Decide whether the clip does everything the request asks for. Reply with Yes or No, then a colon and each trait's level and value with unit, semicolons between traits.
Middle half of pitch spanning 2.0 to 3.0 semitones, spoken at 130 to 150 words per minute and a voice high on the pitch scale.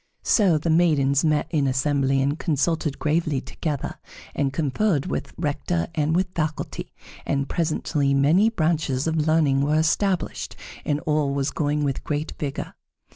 No: average, 2.7 semitones; average, 145 wpm; medium, 150 Hz